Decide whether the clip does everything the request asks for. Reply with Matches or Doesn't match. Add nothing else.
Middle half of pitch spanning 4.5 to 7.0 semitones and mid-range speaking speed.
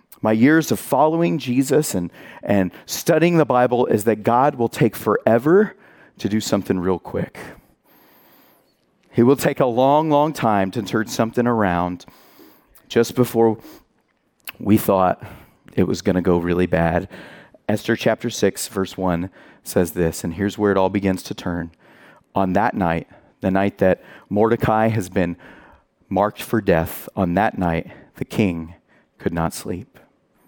Matches